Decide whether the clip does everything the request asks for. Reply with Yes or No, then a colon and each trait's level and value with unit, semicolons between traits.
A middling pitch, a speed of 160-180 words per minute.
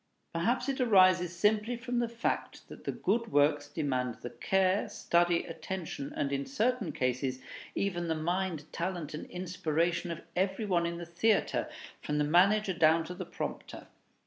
Yes: medium, 175 Hz; average, 165 wpm